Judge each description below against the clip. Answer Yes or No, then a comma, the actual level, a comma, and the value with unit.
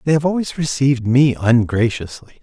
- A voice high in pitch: No, low, 130 Hz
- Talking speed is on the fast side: No, average, 150 wpm